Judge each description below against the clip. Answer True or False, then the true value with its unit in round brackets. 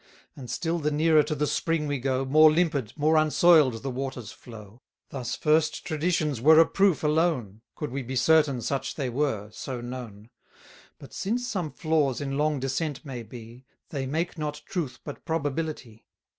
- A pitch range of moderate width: True (3.8 semitones)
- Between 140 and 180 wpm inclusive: True (175 wpm)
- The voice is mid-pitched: True (145 Hz)